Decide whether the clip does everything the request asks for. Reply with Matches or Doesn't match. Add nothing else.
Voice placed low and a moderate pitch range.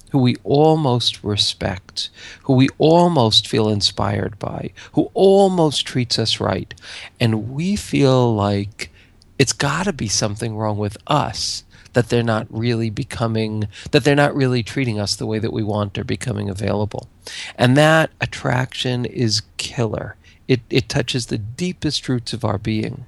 Matches